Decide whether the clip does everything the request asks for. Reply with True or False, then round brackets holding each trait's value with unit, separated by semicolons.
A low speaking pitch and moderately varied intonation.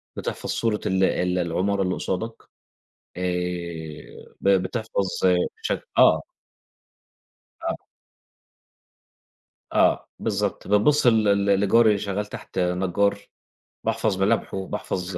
False (95 Hz; 2.2 semitones)